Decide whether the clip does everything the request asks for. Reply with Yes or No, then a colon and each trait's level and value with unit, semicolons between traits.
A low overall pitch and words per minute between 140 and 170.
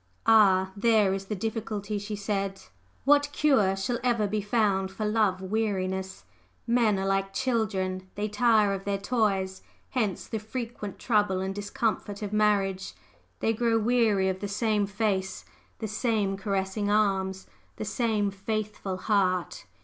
No: high, 205 Hz; average, 150 wpm